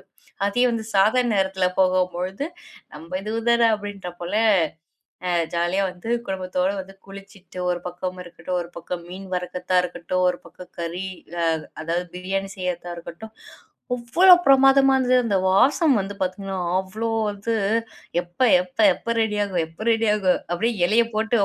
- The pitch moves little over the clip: No, average, 3.6 semitones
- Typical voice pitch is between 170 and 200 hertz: Yes, high, 190 Hz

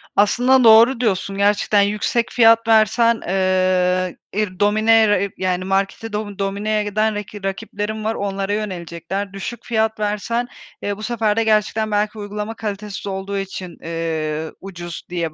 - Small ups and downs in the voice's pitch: Yes, narrow, 2.3 semitones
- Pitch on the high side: Yes, high, 205 Hz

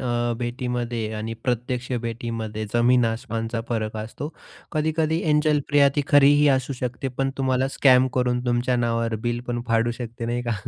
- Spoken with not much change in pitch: Yes, narrow, 2.3 semitones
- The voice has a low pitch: Yes, low, 120 Hz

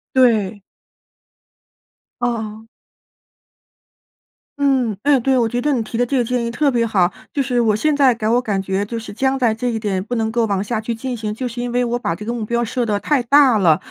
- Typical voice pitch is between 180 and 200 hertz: No, high, 235 Hz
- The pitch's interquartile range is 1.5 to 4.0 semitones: Yes, narrow, 2.6 semitones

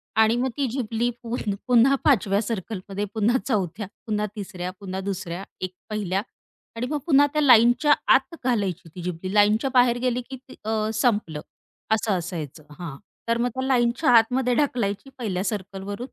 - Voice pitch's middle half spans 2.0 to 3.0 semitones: No, average, 4.2 semitones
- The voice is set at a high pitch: Yes, high, 220 Hz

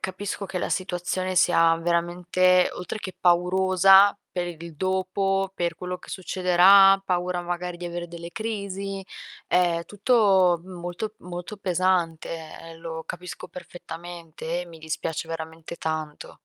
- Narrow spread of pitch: Yes, narrow, 1.8 semitones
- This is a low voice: No, medium, 180 Hz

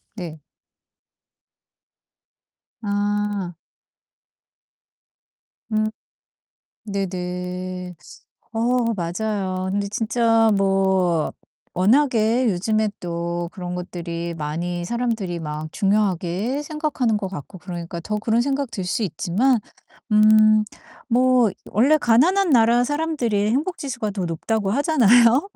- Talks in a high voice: Yes, high, 210 Hz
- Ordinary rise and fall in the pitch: Yes, average, 4.8 semitones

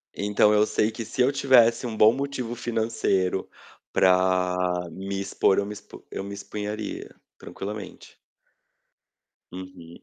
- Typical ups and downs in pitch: Yes, average, 3.1 semitones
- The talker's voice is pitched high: No, low, 105 Hz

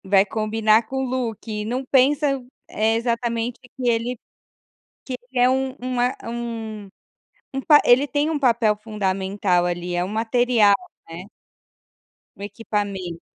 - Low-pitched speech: No, high, 230 Hz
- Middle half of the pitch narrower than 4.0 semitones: Yes, average, 3.4 semitones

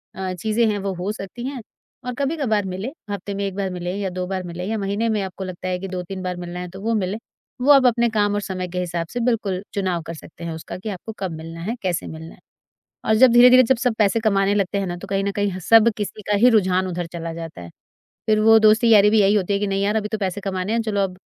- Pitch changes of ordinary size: Yes, average, 3.1 semitones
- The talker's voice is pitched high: Yes, high, 195 Hz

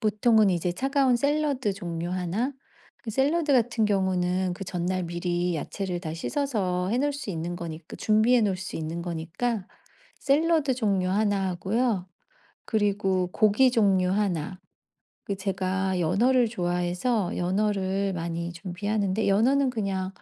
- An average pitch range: Yes, average, 4.4 semitones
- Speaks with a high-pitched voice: Yes, high, 195 Hz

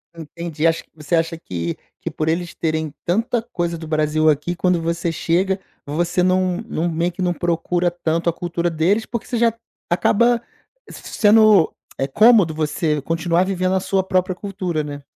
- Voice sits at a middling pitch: Yes, medium, 175 Hz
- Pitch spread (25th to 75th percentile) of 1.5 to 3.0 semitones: Yes, narrow, 2.6 semitones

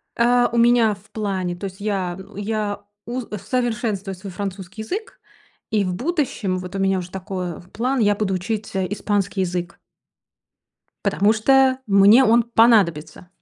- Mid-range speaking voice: No, high, 205 Hz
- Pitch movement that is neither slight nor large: Yes, average, 3.6 semitones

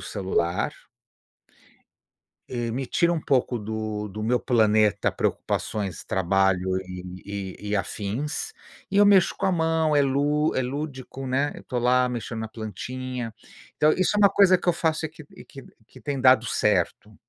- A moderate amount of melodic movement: No, wide, 6.0 semitones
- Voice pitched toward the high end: No, low, 125 Hz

